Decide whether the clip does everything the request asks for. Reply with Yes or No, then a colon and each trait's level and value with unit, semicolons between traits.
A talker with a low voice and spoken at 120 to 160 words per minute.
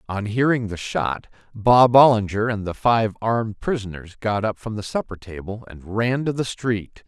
No: low, 110 Hz; average, 185 wpm